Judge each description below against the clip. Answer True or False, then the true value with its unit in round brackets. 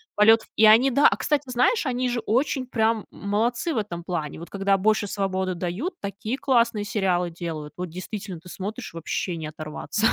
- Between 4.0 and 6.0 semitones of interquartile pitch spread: True (4.8 semitones)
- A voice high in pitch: True (205 Hz)